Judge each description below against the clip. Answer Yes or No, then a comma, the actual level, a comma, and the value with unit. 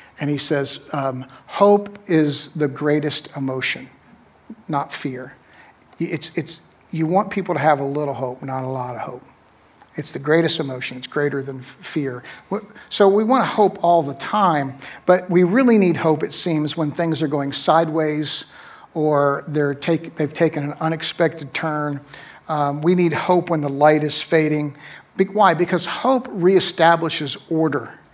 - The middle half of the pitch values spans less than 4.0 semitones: Yes, average, 3.2 semitones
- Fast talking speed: No, average, 165 wpm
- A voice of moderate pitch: Yes, medium, 155 Hz